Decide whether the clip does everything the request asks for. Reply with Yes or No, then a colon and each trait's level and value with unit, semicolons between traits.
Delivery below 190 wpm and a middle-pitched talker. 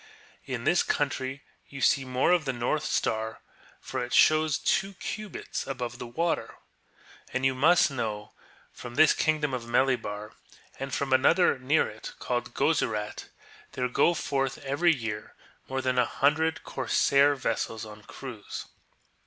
No: average, 150 wpm; low, 130 Hz